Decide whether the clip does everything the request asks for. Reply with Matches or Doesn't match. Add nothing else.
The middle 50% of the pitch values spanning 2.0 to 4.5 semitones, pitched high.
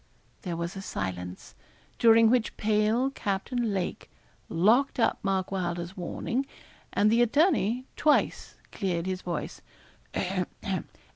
Doesn't match